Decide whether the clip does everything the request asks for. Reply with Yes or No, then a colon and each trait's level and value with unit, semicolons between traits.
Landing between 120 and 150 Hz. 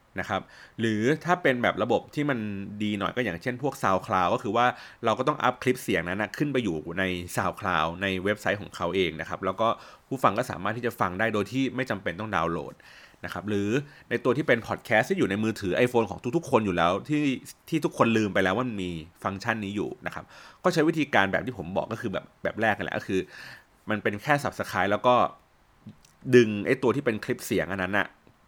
No: low, 110 Hz